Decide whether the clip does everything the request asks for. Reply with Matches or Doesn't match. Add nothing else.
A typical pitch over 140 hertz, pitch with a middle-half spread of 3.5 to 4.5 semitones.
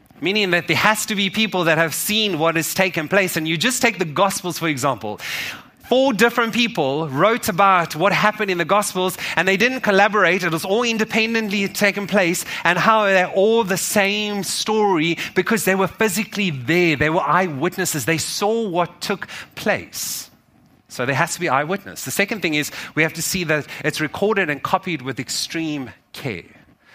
Matches